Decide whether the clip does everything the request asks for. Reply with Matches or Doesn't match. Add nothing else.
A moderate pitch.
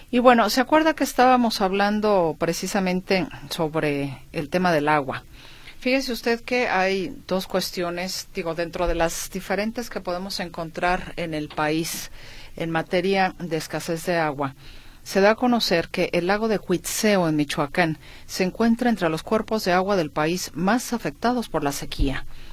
Matches